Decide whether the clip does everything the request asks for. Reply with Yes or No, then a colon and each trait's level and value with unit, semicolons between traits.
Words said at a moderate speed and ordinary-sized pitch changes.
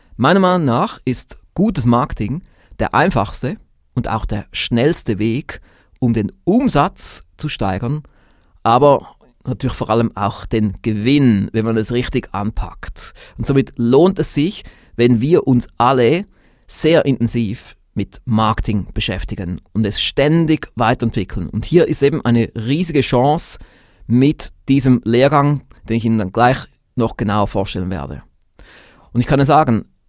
Yes: average, 145 wpm; average, 4.1 semitones